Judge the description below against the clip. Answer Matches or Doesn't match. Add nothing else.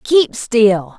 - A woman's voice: Matches